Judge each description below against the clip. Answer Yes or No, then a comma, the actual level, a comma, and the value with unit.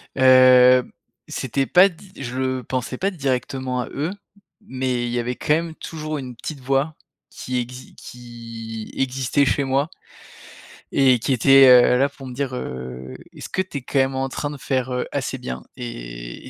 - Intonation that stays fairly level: Yes, narrow, 2.1 semitones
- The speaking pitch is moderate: No, low, 130 Hz